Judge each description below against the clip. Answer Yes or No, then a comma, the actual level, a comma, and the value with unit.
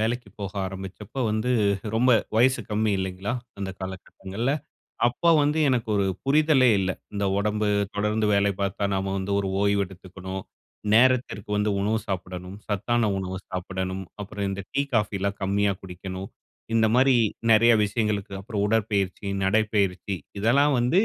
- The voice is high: No, low, 100 Hz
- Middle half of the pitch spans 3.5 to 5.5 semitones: No, average, 2.9 semitones